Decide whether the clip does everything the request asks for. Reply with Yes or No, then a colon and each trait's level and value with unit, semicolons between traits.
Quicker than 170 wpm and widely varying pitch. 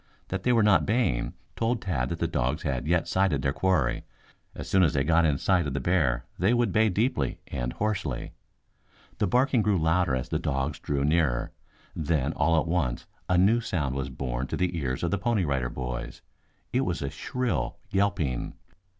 Yes: average, 200 wpm; wide, 6.2 semitones